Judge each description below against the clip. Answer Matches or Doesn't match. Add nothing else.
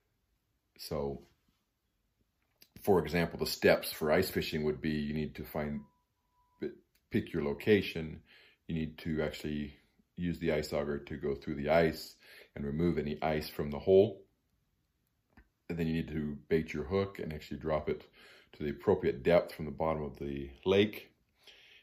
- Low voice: Matches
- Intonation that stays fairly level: Matches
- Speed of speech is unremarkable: Matches